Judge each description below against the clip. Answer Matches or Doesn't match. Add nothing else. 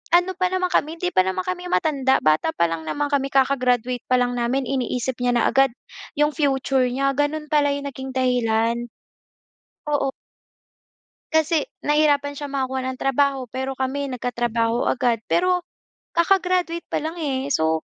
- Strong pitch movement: Doesn't match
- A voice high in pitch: Matches